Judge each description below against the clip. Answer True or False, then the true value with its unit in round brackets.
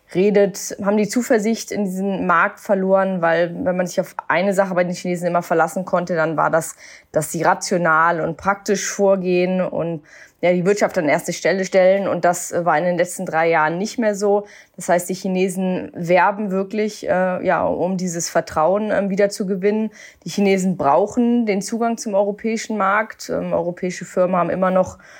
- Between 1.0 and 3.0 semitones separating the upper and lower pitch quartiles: True (2.4 semitones)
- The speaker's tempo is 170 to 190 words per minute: True (185 wpm)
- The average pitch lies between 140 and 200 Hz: True (190 Hz)